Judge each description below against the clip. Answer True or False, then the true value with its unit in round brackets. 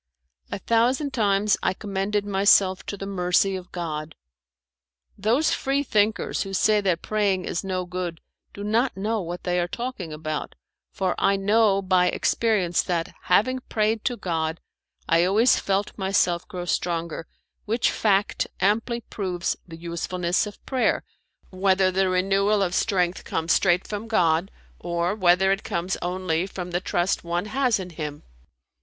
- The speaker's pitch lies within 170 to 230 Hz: True (190 Hz)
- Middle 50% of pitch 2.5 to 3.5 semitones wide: True (3.0 semitones)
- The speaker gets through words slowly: False (155 wpm)